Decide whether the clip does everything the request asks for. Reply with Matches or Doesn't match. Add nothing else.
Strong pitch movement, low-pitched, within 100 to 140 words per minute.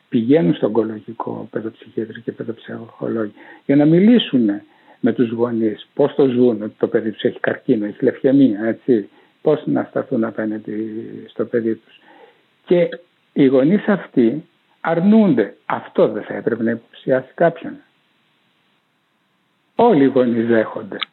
Matches